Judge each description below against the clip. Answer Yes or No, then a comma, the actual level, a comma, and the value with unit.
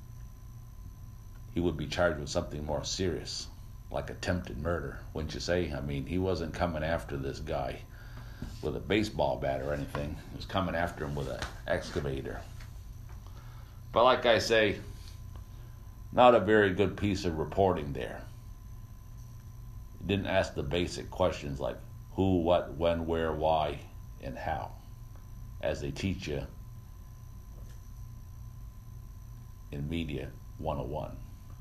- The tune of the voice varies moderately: Yes, average, 4.6 semitones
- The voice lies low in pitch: Yes, low, 100 Hz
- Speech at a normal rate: No, slow, 130 wpm